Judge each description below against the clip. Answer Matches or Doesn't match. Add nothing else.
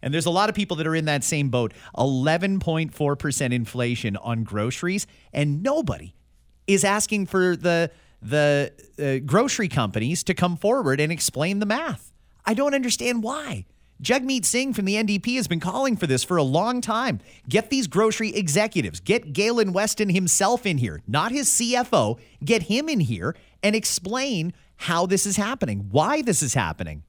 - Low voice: Doesn't match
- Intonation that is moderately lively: Doesn't match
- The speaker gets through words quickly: Doesn't match